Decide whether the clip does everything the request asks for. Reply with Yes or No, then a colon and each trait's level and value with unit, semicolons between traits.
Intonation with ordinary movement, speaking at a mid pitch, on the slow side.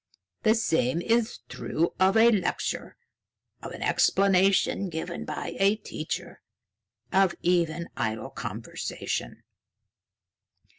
Yes: average, 3.7 semitones; medium, 180 Hz; slow, 100 wpm